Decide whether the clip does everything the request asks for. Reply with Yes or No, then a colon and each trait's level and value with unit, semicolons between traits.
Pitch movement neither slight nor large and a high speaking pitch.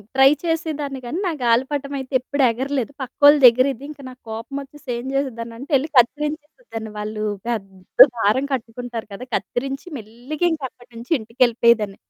Yes: average, 3.6 semitones; very high, 255 Hz